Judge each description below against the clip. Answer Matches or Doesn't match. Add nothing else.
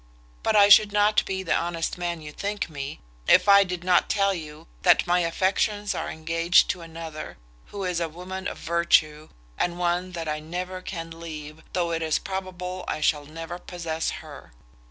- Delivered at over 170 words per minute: Matches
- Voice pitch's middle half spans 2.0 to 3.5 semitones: Matches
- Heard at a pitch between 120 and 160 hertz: Doesn't match